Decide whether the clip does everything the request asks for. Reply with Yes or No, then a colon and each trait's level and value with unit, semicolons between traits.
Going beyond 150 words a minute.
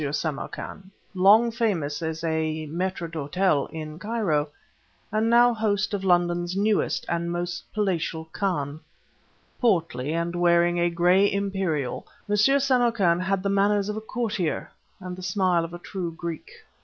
No: average, 145 wpm